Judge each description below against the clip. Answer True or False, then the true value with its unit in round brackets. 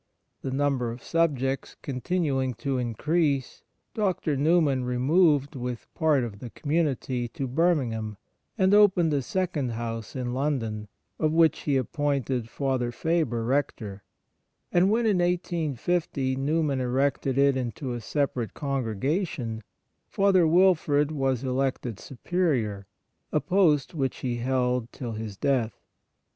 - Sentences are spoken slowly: True (125 wpm)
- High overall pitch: False (135 Hz)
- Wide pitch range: False (4.5 semitones)